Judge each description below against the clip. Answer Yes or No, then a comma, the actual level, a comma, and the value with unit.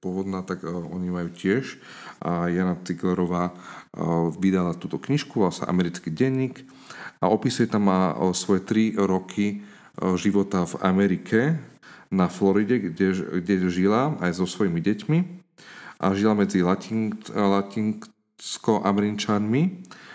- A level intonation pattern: No, average, 3.1 semitones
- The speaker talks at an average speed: No, slow, 105 wpm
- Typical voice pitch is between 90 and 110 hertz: Yes, low, 100 Hz